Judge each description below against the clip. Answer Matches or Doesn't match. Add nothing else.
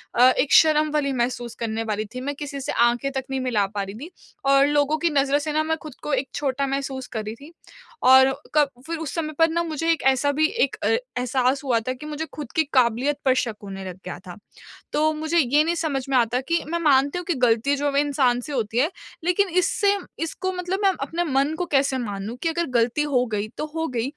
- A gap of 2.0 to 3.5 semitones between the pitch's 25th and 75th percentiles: Doesn't match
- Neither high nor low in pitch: Doesn't match